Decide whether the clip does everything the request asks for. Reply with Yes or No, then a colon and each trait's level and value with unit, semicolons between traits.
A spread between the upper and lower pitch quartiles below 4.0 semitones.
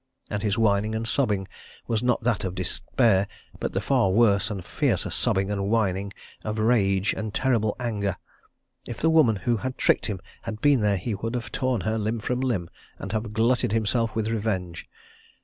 Yes: average, 2.8 semitones